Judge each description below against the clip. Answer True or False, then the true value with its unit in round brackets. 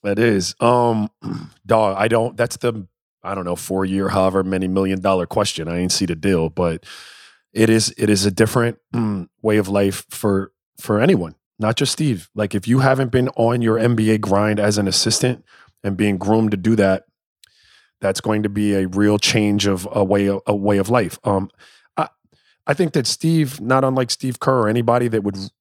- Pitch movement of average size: True (3.3 semitones)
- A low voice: True (105 Hz)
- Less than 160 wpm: False (200 wpm)